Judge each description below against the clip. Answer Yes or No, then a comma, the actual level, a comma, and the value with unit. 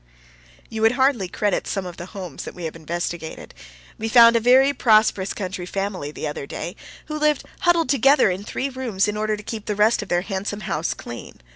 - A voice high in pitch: Yes, high, 210 Hz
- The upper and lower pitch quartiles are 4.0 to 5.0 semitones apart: Yes, average, 4.6 semitones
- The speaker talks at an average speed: No, fast, 210 wpm